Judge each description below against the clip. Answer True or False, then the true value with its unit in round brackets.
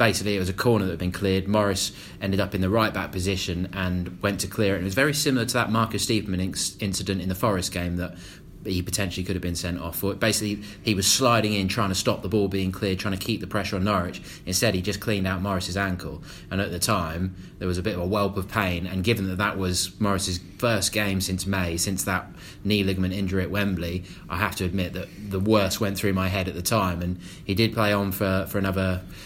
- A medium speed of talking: False (250 wpm)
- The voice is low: True (95 Hz)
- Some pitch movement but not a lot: False (2.0 semitones)